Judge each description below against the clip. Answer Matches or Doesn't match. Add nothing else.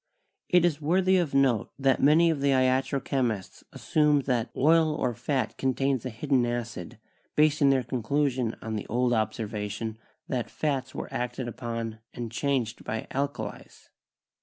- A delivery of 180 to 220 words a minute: Doesn't match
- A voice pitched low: Matches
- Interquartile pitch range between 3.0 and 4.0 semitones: Matches